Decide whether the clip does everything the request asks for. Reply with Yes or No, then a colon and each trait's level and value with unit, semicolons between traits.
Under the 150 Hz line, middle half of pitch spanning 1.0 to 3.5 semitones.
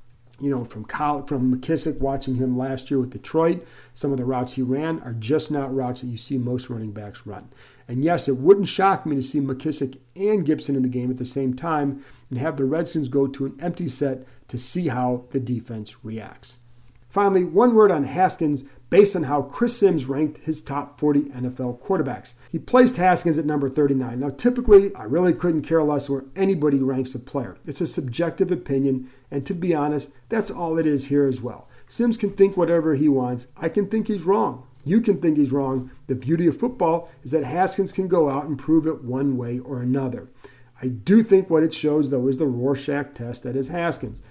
No: medium, 140 Hz; average, 4.4 semitones